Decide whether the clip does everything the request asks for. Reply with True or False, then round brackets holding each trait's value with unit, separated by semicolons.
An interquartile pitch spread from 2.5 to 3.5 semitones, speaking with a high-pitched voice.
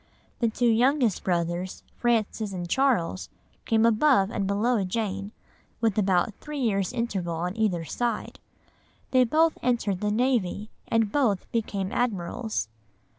False (4.1 semitones; 215 Hz)